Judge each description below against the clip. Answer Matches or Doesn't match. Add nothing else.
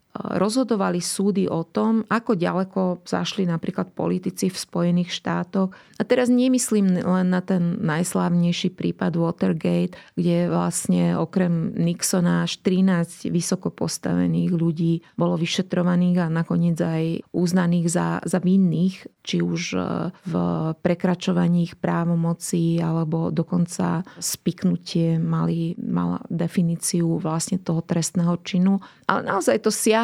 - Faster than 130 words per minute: Doesn't match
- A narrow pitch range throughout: Matches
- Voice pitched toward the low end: Doesn't match